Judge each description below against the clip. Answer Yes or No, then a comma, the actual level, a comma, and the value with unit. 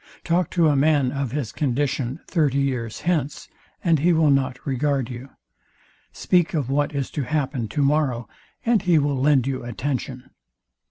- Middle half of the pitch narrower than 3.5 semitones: Yes, average, 2.9 semitones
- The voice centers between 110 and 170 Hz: Yes, medium, 140 Hz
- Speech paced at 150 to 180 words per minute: Yes, average, 160 wpm